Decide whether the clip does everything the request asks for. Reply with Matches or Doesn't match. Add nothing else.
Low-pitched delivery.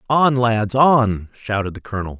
Matches